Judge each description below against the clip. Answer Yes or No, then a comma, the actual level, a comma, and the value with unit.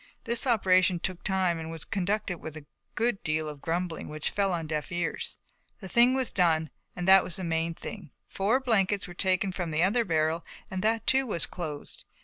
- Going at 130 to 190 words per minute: No, average, 200 wpm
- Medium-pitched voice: Yes, medium, 180 Hz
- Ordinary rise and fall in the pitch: Yes, average, 3.7 semitones